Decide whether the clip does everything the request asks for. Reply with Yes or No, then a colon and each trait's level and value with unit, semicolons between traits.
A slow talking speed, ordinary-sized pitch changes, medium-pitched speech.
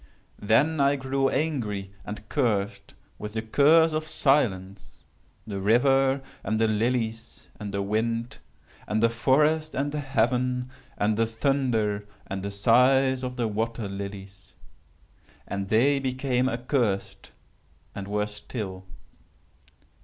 No: slow, 125 wpm; average, 4.4 semitones; low, 115 Hz